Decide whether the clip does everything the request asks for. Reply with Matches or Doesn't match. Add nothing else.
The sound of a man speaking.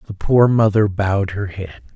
Matches